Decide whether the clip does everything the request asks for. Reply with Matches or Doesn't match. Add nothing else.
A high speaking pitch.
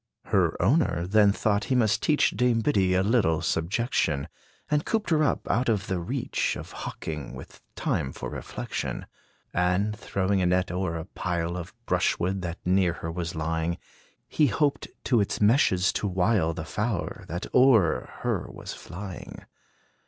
Doesn't match